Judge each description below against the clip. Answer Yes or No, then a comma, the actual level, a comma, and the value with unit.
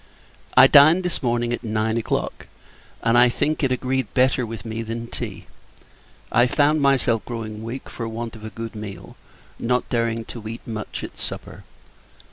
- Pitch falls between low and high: No, low, 115 Hz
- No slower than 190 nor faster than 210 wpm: No, average, 170 wpm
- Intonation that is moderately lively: No, narrow, 2.3 semitones